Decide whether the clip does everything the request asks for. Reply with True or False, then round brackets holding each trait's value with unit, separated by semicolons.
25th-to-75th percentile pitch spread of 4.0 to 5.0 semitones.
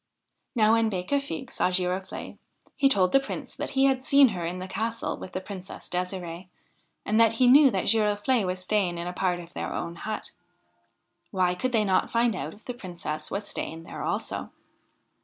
True (4.3 semitones)